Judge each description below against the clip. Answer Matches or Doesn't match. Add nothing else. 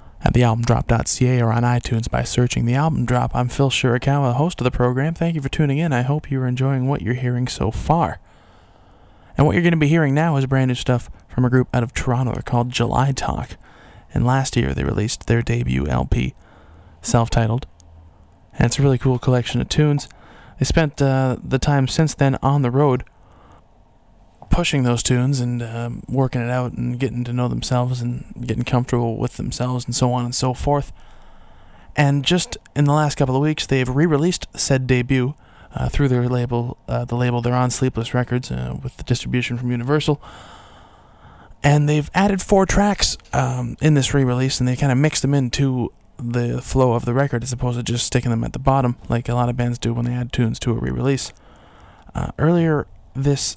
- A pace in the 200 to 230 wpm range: Matches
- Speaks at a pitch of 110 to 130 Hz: Matches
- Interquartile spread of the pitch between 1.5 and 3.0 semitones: Matches